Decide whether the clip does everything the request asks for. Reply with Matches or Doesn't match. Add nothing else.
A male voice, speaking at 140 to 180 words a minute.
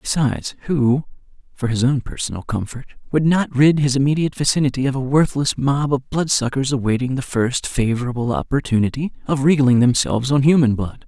Matches